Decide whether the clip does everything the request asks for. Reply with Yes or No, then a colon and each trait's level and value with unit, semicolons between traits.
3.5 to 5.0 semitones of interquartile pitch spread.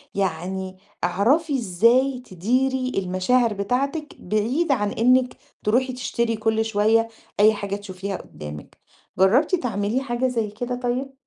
Yes: average, 4.3 semitones